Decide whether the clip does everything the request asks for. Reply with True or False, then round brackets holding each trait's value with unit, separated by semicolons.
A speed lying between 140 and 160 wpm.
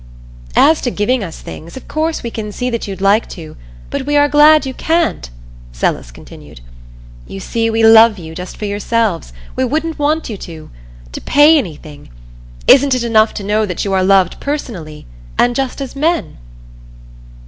False (180 wpm)